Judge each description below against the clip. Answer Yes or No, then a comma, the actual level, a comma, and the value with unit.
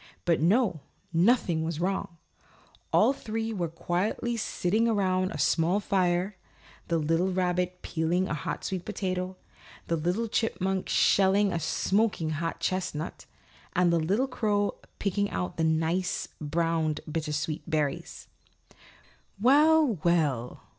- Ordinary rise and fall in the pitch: Yes, average, 3.7 semitones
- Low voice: No, medium, 180 Hz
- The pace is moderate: No, slow, 125 wpm